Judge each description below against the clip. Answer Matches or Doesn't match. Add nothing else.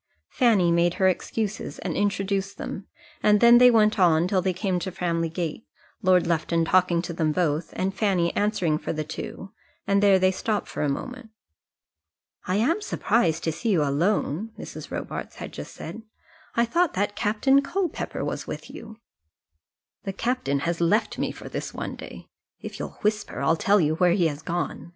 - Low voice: Doesn't match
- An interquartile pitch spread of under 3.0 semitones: Doesn't match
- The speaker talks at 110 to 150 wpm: Doesn't match